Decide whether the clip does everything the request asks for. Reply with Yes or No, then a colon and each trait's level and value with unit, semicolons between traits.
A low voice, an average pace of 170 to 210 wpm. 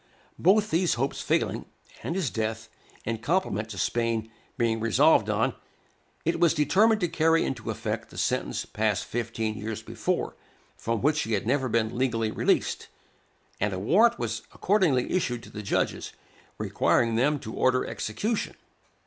No: low, 120 Hz; average, 155 wpm